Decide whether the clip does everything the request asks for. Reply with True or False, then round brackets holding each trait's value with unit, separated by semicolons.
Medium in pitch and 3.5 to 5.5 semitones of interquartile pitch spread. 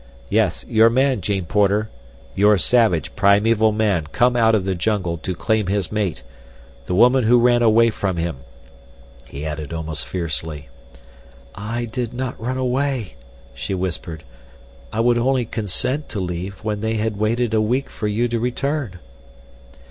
False (105 Hz; 4.5 semitones)